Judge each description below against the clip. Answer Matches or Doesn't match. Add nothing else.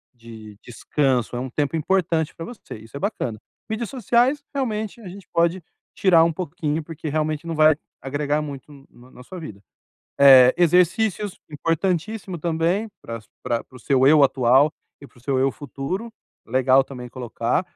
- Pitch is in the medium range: Matches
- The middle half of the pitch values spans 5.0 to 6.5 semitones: Matches